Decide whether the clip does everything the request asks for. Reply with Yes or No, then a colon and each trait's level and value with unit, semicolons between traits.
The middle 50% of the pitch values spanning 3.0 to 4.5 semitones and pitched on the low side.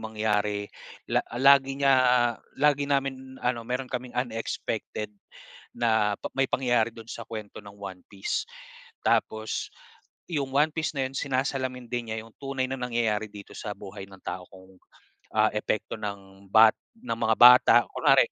Yes: average, 4.0 semitones; low, 115 Hz